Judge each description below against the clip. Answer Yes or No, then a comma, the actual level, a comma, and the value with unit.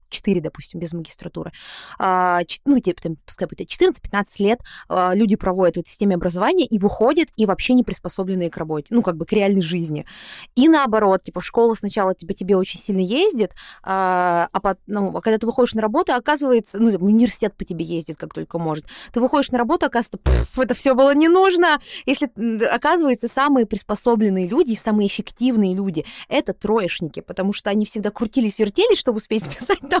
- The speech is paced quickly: Yes, fast, 180 wpm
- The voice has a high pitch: Yes, high, 210 Hz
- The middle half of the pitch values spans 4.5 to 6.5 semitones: Yes, average, 5.1 semitones